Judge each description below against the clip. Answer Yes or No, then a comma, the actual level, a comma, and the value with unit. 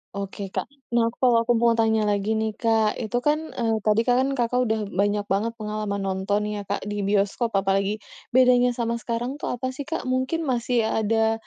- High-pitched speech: Yes, high, 225 Hz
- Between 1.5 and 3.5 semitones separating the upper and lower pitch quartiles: Yes, average, 2.9 semitones